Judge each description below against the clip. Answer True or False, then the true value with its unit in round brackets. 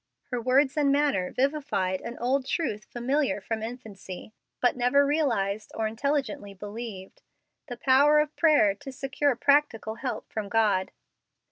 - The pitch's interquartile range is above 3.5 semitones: True (4.8 semitones)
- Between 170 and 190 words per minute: False (140 wpm)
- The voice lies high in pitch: True (245 Hz)